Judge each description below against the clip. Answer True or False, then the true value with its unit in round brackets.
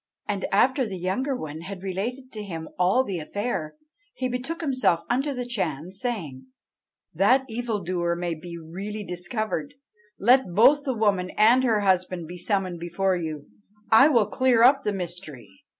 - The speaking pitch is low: False (200 Hz)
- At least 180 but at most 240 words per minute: False (165 wpm)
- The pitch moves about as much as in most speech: False (6.0 semitones)